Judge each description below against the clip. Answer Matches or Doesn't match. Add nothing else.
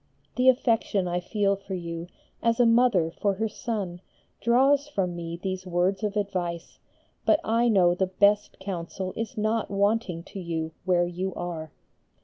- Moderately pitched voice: Doesn't match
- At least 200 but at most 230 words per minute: Doesn't match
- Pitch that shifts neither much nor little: Matches